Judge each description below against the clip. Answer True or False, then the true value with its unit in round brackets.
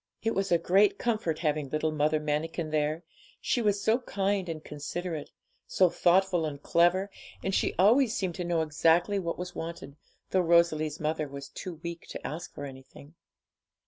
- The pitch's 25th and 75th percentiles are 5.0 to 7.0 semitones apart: False (3.7 semitones)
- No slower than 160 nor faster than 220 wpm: True (175 wpm)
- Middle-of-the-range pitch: True (170 Hz)